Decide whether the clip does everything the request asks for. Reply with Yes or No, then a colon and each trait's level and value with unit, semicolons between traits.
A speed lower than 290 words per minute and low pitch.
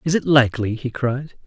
Yes: fast, 205 wpm; low, 130 Hz